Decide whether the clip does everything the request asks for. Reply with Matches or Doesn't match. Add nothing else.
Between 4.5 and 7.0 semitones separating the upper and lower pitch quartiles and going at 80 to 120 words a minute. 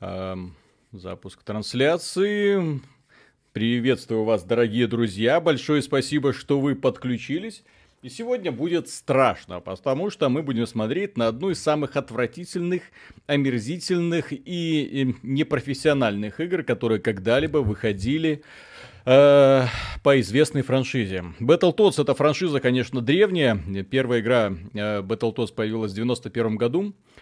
Matches